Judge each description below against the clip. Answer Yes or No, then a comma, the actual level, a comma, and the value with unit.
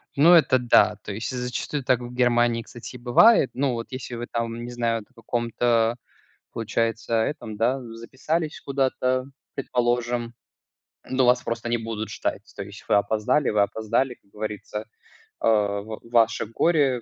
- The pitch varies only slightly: Yes, narrow, 2.2 semitones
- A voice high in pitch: No, low, 120 Hz